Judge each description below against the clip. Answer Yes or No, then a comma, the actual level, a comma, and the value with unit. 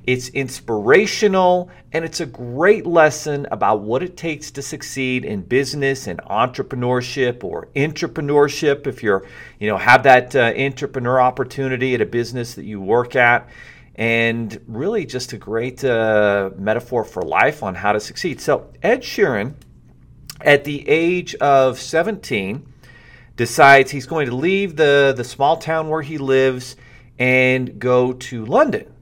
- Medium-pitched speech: No, low, 130 Hz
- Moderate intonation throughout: Yes, average, 3.2 semitones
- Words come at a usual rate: Yes, average, 150 wpm